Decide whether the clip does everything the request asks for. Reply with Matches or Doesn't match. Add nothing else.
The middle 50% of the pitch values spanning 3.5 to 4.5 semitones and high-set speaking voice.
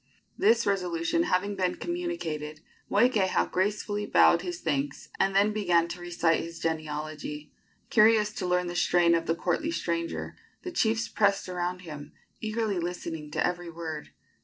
Doesn't match